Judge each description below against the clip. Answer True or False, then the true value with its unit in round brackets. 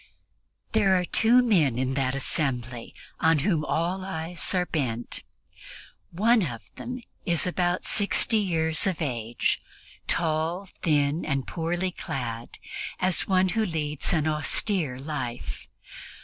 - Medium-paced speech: False (125 wpm)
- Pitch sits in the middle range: True (160 Hz)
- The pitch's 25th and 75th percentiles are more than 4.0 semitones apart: True (5.2 semitones)